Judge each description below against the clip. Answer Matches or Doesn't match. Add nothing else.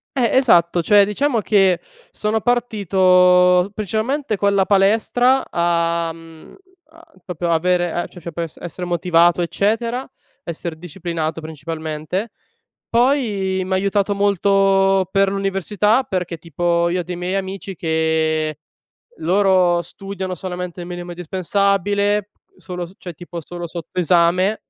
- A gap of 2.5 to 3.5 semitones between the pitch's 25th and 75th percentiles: Matches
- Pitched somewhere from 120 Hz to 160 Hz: Doesn't match